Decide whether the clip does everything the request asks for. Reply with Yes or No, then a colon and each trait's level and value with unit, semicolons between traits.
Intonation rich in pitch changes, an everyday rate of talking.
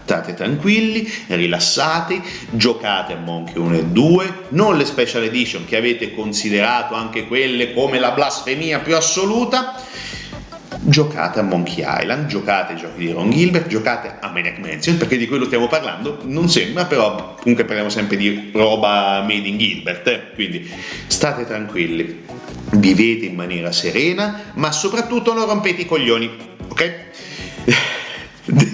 Yes: wide, 8.4 semitones; average, 140 wpm